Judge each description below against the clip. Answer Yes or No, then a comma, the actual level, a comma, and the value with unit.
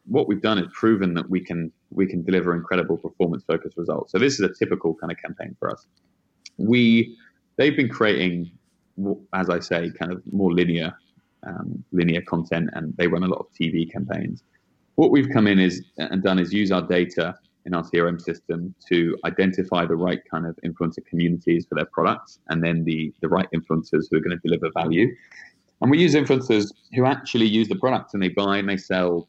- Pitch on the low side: Yes, very low, 90 Hz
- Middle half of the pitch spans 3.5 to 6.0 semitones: No, average, 2.9 semitones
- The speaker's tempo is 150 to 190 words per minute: No, fast, 205 wpm